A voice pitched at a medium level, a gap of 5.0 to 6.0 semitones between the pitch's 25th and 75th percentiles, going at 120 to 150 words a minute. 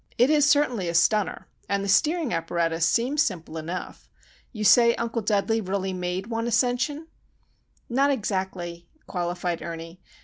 No: high, 200 Hz; wide, 5.6 semitones; average, 140 wpm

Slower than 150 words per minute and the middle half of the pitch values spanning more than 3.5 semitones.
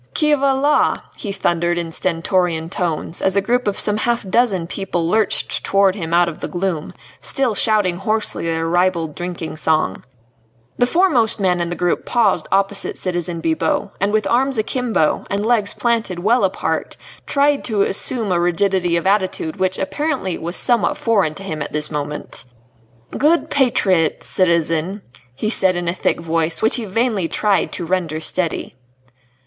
No: average, 165 wpm; average, 4.4 semitones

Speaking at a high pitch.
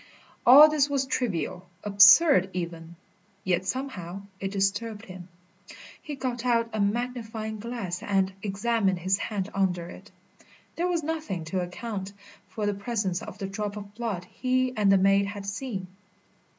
Yes: high, 205 Hz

